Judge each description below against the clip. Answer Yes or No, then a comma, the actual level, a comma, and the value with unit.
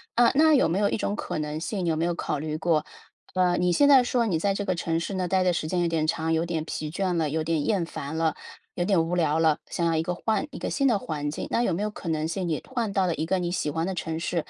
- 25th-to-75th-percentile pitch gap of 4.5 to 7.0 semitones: No, average, 3.3 semitones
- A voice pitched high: No, medium, 170 Hz